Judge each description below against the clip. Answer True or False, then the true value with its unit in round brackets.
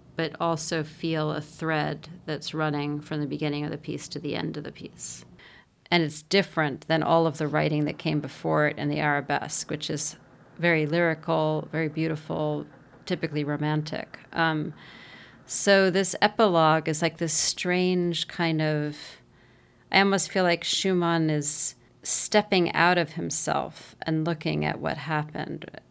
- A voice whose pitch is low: False (160 Hz)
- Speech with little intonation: True (2.1 semitones)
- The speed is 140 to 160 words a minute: True (155 wpm)